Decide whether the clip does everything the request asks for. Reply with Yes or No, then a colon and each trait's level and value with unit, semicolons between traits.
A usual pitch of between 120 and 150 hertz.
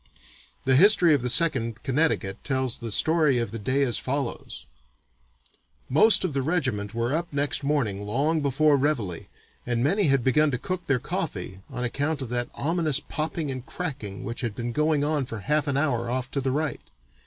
Yes: low, 135 Hz